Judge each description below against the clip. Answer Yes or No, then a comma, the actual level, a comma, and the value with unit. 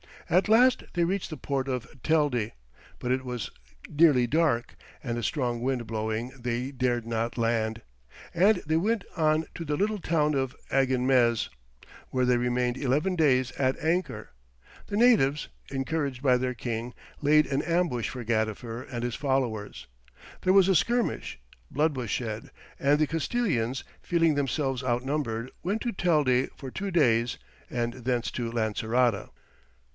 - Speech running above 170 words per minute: No, average, 155 wpm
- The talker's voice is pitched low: Yes, low, 130 Hz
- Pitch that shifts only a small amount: No, average, 4.8 semitones